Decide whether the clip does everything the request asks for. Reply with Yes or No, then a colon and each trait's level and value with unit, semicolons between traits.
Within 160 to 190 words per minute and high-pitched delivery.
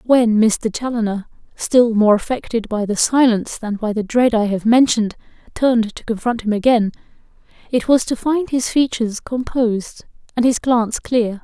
Yes: average, 170 wpm; high, 230 Hz